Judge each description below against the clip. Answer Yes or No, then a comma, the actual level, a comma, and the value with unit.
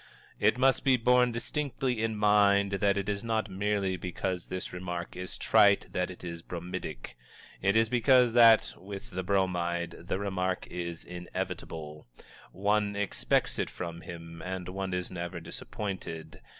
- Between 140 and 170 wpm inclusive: Yes, average, 155 wpm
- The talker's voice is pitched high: No, very low, 95 Hz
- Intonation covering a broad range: No, average, 3.1 semitones